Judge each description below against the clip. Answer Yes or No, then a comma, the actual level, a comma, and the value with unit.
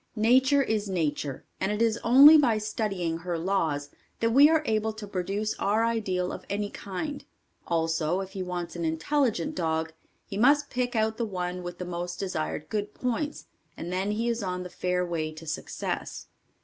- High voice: Yes, high, 195 Hz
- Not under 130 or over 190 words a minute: Yes, average, 185 wpm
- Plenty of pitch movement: No, average, 4.6 semitones